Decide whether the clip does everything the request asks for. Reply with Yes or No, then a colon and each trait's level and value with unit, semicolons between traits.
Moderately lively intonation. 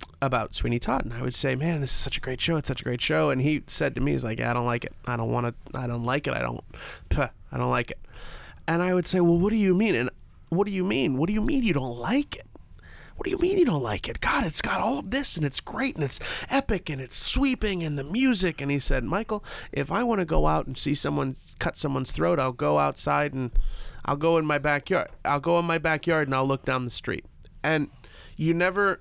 No: wide, 6.2 semitones